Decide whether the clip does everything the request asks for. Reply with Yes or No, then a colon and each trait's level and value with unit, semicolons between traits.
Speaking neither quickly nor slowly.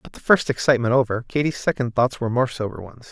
No: fast, 230 wpm